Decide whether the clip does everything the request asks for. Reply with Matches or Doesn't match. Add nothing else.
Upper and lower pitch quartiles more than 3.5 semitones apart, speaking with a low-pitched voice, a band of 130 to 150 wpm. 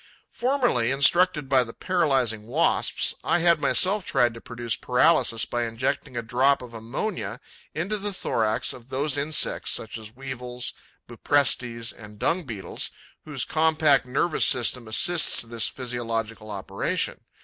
Matches